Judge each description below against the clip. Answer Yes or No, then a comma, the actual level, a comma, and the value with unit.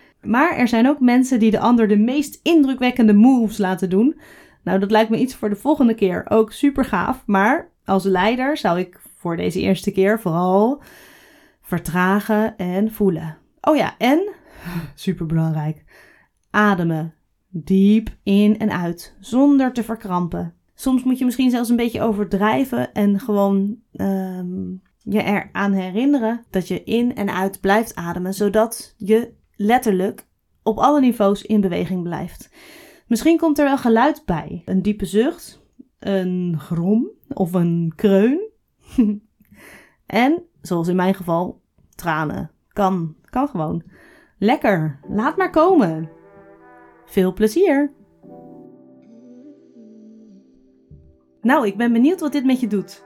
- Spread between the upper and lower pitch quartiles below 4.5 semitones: No, average, 5.3 semitones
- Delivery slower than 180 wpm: Yes, slow, 135 wpm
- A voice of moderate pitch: No, high, 210 Hz